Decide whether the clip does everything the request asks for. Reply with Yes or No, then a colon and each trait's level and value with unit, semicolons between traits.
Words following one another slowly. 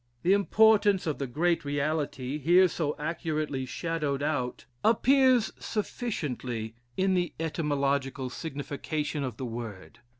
Yes: slow, 120 wpm